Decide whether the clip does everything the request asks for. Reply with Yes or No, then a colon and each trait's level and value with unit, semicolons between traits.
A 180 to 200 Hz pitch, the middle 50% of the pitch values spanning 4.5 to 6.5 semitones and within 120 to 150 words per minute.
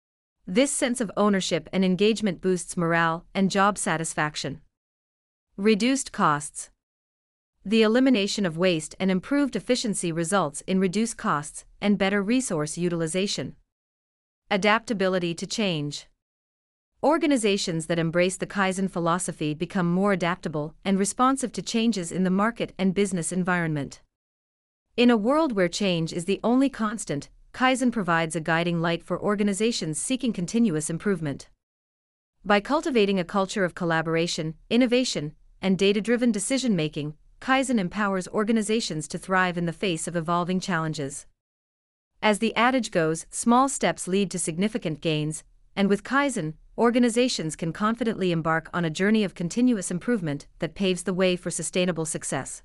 Yes: medium, 185 Hz; average, 4.8 semitones; average, 140 wpm